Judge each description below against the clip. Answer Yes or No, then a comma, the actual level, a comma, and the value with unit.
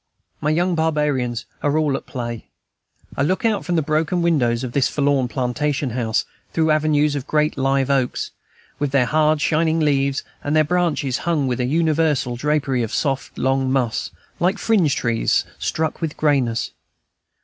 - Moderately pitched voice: Yes, medium, 145 Hz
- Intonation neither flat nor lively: Yes, average, 3.1 semitones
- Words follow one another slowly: No, average, 165 wpm